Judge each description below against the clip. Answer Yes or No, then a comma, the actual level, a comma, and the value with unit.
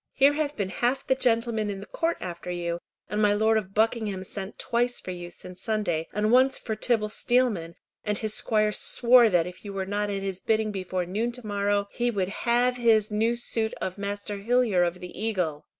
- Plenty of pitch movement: No, average, 3.7 semitones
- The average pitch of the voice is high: Yes, high, 210 Hz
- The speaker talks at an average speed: No, fast, 210 wpm